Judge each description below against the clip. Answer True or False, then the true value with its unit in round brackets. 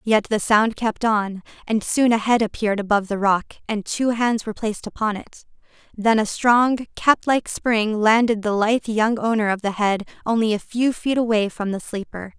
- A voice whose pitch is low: False (220 Hz)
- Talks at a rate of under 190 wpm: False (200 wpm)